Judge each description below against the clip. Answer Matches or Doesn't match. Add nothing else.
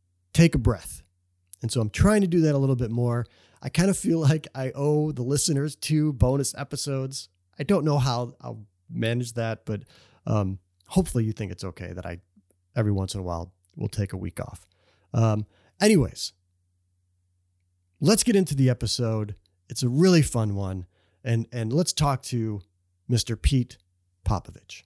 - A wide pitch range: Matches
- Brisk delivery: Doesn't match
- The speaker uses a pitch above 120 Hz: Doesn't match